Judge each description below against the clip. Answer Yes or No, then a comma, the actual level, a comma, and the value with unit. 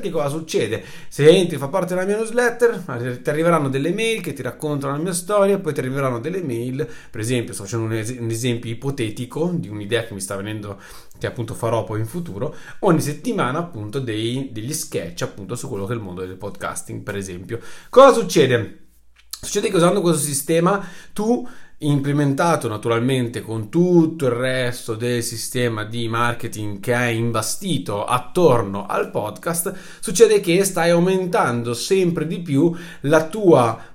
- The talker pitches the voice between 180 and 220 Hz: No, low, 130 Hz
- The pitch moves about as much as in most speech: No, wide, 6.6 semitones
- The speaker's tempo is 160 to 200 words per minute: Yes, fast, 170 wpm